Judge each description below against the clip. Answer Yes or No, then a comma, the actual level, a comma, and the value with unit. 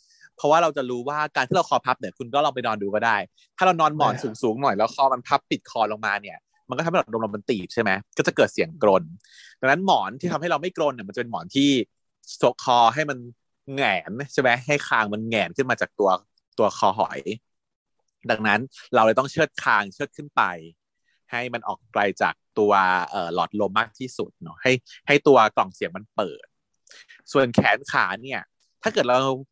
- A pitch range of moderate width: Yes, average, 4.0 semitones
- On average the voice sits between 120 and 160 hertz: Yes, low, 130 Hz